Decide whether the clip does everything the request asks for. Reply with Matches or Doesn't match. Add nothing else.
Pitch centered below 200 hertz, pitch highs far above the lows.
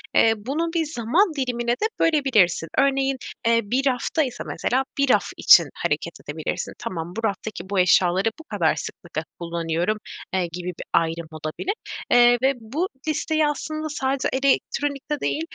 Doesn't match